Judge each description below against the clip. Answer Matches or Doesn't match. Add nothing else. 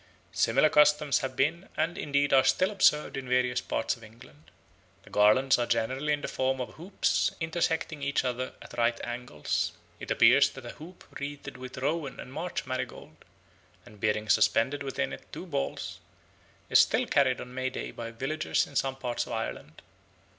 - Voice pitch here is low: Matches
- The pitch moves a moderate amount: Matches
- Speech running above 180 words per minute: Doesn't match